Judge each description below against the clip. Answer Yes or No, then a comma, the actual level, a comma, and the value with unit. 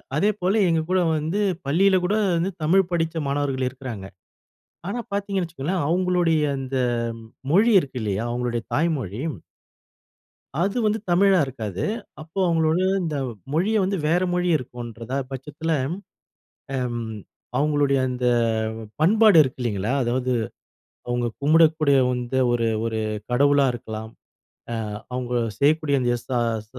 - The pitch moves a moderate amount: No, wide, 6.2 semitones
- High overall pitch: No, medium, 145 Hz